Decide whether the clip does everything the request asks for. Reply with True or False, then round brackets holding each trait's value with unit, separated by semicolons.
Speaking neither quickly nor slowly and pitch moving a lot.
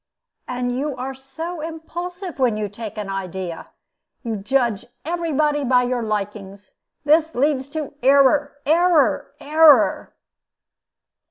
False (120 wpm; 5.7 semitones)